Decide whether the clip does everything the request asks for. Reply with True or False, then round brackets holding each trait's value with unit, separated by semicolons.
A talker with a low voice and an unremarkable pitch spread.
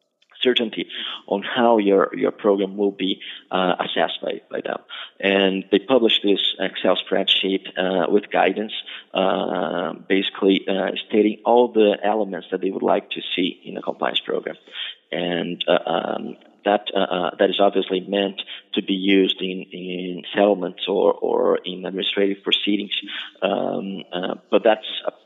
False (100 Hz; 1.8 semitones)